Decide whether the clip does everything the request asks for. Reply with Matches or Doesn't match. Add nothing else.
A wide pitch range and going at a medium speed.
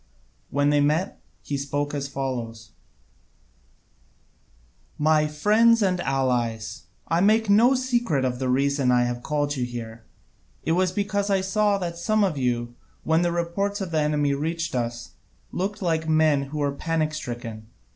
Matches